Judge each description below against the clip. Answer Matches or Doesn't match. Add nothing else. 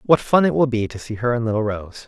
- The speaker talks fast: Matches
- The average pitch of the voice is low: Matches